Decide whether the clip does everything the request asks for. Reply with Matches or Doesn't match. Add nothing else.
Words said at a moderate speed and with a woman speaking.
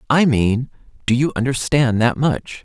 Doesn't match